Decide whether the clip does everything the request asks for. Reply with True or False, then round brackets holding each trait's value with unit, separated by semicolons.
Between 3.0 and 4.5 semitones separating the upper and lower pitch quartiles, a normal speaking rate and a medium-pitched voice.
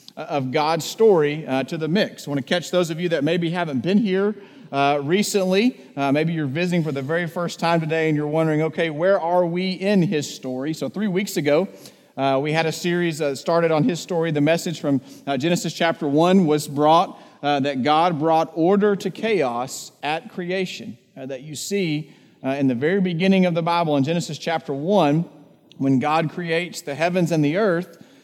False (3.5 semitones; 210 wpm; 165 Hz)